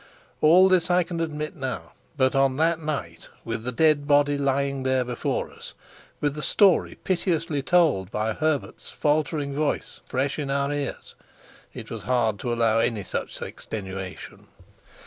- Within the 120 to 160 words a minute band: Yes, average, 155 wpm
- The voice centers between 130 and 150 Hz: Yes, medium, 140 Hz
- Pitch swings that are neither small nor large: Yes, average, 3.9 semitones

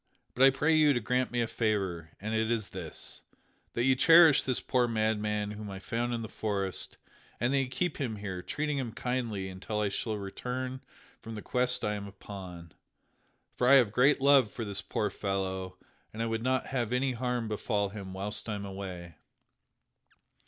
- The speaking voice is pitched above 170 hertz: No, low, 110 Hz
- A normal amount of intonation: Yes, average, 4.0 semitones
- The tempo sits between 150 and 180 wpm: No, average, 195 wpm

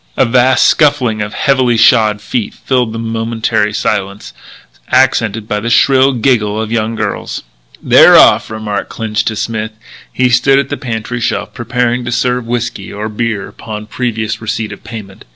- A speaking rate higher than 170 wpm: No, average, 165 wpm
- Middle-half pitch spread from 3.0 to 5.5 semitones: No, narrow, 2.4 semitones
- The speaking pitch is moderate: No, low, 115 Hz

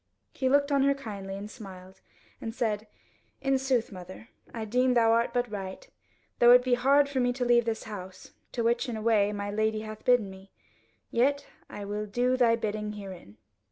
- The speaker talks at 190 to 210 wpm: Yes, average, 195 wpm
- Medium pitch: No, high, 225 Hz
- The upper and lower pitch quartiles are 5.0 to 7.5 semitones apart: No, average, 3.3 semitones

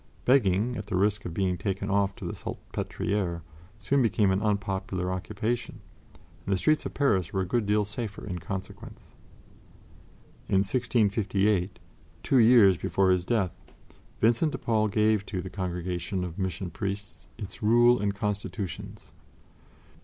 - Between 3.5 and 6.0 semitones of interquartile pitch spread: No, narrow, 2.6 semitones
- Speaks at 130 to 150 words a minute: Yes, average, 145 wpm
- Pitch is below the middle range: Yes, low, 100 Hz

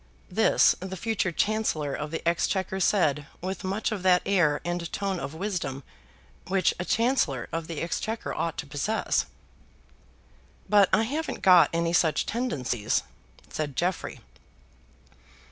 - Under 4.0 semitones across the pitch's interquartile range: No, average, 4.3 semitones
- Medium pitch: Yes, medium, 180 Hz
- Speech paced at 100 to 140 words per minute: Yes, slow, 135 wpm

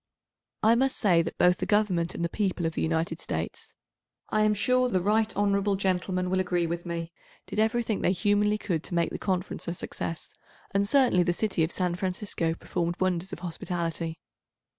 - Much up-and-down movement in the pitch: No, average, 3.4 semitones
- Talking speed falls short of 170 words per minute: No, average, 185 wpm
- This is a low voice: No, medium, 185 Hz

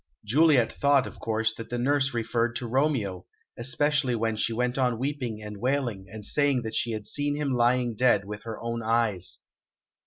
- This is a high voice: No, low, 120 Hz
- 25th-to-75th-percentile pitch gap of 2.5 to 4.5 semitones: Yes, average, 3.2 semitones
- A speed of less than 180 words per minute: No, average, 185 wpm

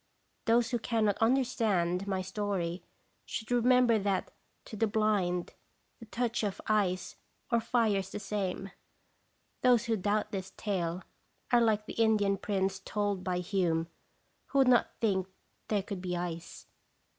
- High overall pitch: Yes, high, 205 Hz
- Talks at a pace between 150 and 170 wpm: Yes, average, 155 wpm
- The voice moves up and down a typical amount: Yes, average, 3.3 semitones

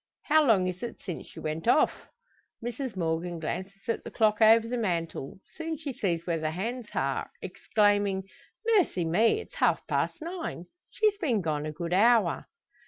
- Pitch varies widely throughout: Yes, wide, 6.2 semitones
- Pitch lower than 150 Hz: No, high, 205 Hz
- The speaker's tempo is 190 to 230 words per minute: No, average, 170 wpm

